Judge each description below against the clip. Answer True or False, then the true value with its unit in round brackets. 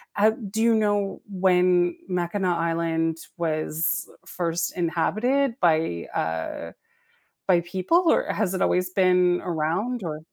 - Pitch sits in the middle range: True (180 Hz)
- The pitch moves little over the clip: False (3.3 semitones)